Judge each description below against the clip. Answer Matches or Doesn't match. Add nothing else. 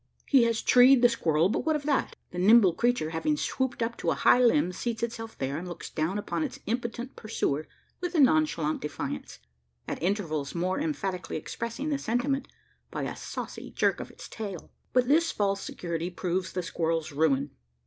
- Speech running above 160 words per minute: Matches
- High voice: Matches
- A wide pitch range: Matches